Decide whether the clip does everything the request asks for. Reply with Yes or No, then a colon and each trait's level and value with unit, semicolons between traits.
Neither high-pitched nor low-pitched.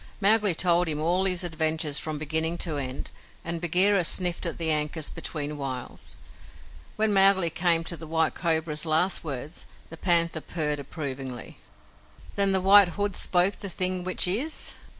Yes: medium, 170 Hz